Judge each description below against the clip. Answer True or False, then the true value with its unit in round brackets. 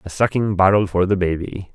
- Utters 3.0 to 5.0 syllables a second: False (5.5 syllables/s)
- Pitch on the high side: False (95 Hz)